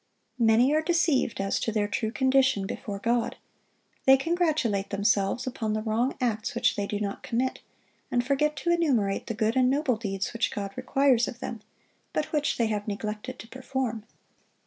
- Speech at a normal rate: Yes, average, 175 wpm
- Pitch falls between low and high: No, high, 235 Hz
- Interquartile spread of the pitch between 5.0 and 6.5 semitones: No, average, 4.0 semitones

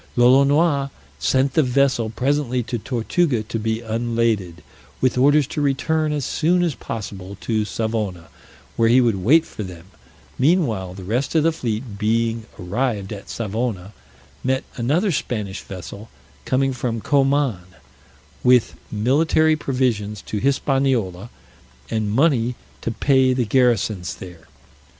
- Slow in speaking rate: Yes, slow, 130 wpm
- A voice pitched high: No, low, 120 Hz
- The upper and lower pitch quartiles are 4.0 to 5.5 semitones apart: Yes, average, 4.4 semitones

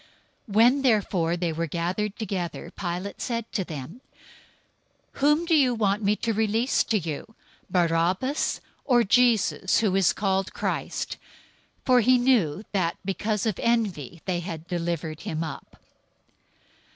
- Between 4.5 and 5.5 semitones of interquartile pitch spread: Yes, average, 5.2 semitones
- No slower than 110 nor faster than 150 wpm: Yes, average, 140 wpm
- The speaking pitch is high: Yes, high, 195 Hz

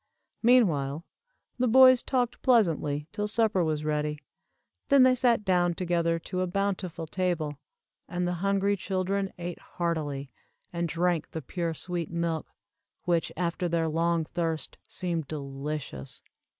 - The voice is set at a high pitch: No, medium, 175 Hz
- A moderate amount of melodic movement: Yes, average, 3.6 semitones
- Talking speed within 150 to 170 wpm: No, slow, 135 wpm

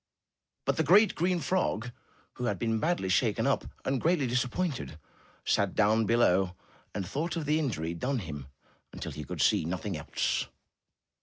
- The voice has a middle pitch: No, low, 120 Hz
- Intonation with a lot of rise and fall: Yes, wide, 8.8 semitones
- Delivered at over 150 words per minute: Yes, average, 160 wpm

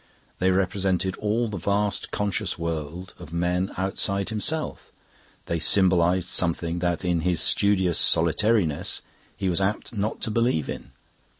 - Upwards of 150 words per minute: No, slow, 135 wpm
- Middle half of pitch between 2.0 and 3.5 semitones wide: Yes, average, 2.8 semitones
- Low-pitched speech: Yes, very low, 95 Hz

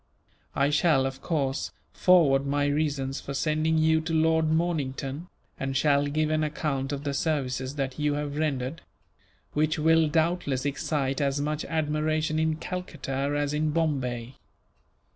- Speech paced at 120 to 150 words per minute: Yes, average, 145 wpm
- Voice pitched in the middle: Yes, medium, 150 Hz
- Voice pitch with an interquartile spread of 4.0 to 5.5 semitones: No, narrow, 2.4 semitones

